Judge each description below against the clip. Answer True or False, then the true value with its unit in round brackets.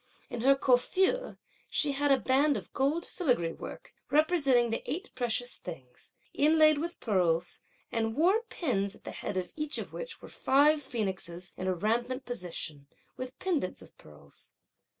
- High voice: True (255 Hz)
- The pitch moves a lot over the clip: True (8.0 semitones)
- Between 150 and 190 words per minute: True (160 wpm)